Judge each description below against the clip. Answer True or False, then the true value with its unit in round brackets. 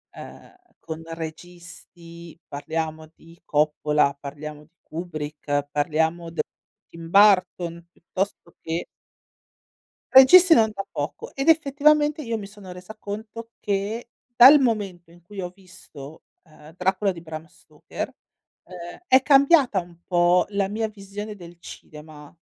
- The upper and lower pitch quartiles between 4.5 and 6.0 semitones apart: True (4.8 semitones)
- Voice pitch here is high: False (180 Hz)